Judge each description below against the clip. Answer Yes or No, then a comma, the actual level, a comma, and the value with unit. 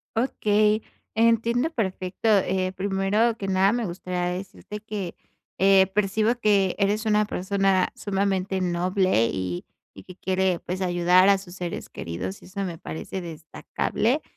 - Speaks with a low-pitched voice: No, high, 195 Hz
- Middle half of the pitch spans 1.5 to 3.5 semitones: Yes, narrow, 2.5 semitones